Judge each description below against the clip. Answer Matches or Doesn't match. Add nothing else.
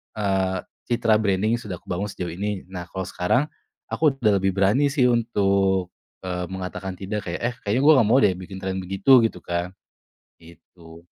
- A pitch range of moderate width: Matches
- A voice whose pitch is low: Matches